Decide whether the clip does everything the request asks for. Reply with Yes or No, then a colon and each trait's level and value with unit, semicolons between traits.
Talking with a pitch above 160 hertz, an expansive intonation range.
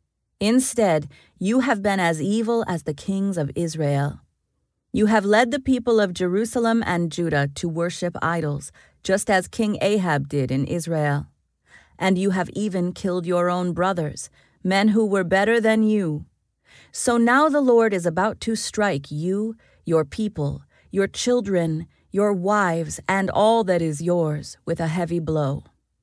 No: medium, 185 Hz; average, 4.5 semitones